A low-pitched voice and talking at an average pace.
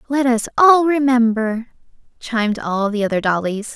No: high, 235 Hz; average, 145 wpm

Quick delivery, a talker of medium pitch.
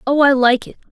No: fast, 260 wpm; very high, 265 Hz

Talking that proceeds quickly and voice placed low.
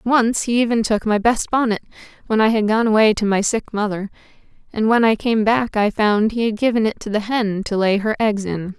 No: fast, 240 wpm; high, 220 Hz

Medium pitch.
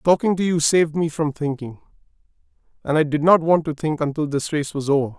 Yes: medium, 155 Hz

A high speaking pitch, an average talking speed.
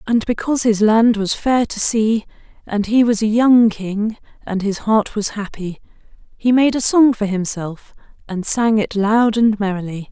Yes: high, 215 Hz; average, 185 wpm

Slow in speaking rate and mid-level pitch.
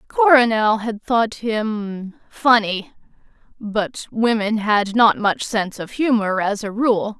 No: slow, 125 wpm; high, 220 Hz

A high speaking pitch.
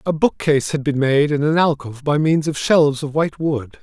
No: medium, 145 Hz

